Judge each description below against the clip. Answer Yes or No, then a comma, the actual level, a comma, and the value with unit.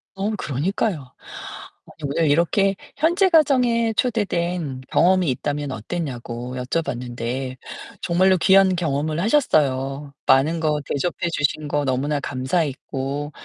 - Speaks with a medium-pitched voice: Yes, medium, 155 Hz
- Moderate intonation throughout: No, wide, 5.7 semitones